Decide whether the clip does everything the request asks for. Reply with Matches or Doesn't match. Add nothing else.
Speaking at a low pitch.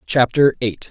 Matches